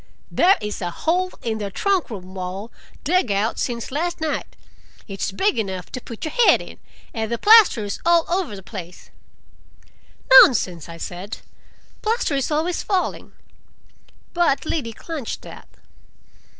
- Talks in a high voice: Yes, high, 235 Hz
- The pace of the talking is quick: No, average, 145 wpm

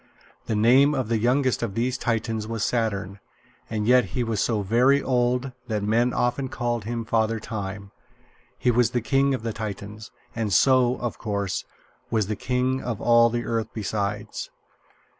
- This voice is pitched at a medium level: No, low, 115 Hz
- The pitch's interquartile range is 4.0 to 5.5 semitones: No, narrow, 2.6 semitones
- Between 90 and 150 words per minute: No, average, 170 wpm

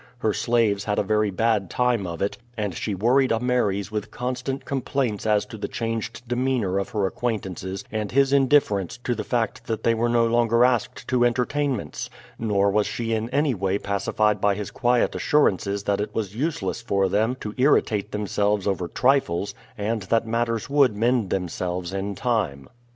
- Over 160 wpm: Yes, average, 180 wpm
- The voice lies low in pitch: Yes, low, 110 Hz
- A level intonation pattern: No, average, 3.4 semitones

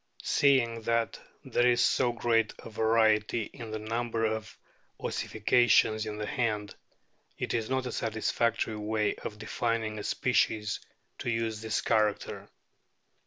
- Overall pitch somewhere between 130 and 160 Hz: No, low, 110 Hz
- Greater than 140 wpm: No, slow, 135 wpm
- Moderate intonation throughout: No, narrow, 1.3 semitones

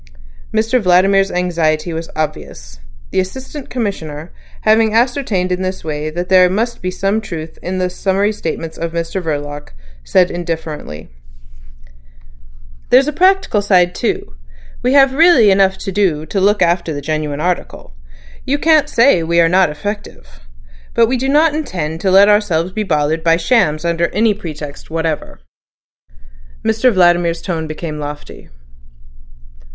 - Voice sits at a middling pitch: Yes, medium, 180 Hz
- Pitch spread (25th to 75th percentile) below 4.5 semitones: No, average, 5.0 semitones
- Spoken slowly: No, average, 145 wpm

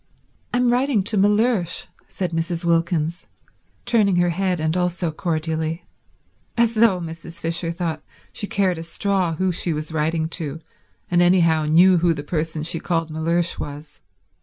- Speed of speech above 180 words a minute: No, average, 150 wpm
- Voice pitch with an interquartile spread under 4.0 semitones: Yes, narrow, 2.6 semitones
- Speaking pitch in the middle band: Yes, medium, 170 Hz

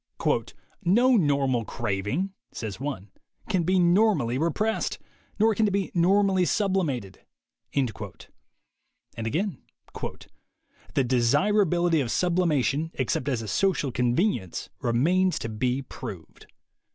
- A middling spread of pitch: No, wide, 7.5 semitones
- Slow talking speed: Yes, slow, 115 wpm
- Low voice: No, medium, 155 Hz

